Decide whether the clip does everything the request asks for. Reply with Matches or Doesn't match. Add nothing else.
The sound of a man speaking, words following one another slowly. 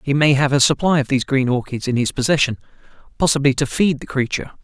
Doesn't match